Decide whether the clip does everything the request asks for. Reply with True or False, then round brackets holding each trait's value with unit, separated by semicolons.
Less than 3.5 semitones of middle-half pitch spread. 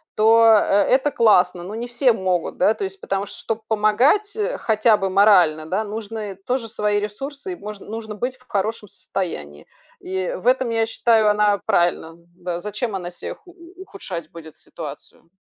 False (4.0 semitones)